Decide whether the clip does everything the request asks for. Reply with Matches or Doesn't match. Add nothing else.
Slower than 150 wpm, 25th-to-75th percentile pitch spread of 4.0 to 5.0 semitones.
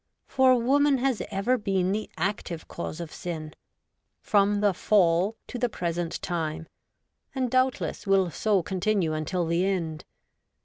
Matches